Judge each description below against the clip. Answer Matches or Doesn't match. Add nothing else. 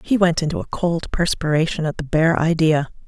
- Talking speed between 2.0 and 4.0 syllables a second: Doesn't match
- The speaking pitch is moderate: Matches